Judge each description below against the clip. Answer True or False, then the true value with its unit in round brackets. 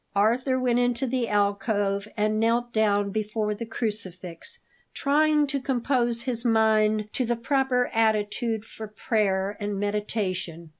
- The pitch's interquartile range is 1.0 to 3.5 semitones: True (2.9 semitones)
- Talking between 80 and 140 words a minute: True (135 wpm)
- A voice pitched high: True (220 Hz)